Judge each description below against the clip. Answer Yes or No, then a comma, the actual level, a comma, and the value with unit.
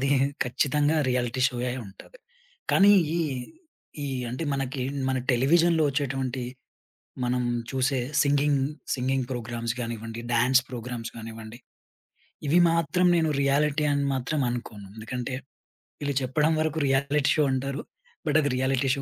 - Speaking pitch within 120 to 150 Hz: Yes, low, 135 Hz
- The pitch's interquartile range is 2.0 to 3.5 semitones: Yes, average, 2.9 semitones